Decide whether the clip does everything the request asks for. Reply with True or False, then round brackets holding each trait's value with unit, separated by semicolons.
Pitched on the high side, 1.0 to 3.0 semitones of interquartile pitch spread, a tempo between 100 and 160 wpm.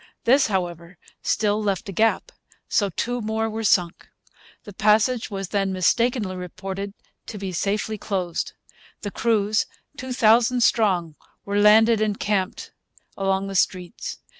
True (205 Hz; 2.6 semitones; 140 wpm)